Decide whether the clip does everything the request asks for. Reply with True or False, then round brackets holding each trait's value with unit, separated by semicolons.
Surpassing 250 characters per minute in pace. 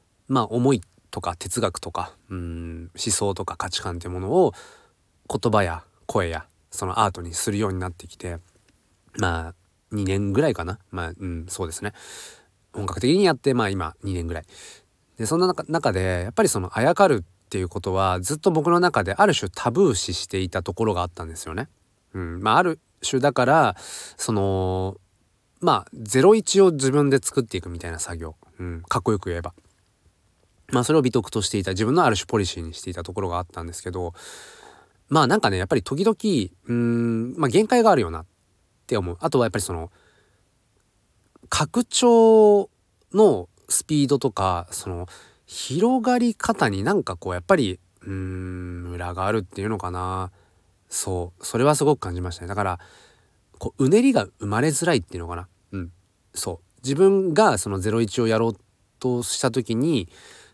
True (340 characters per minute)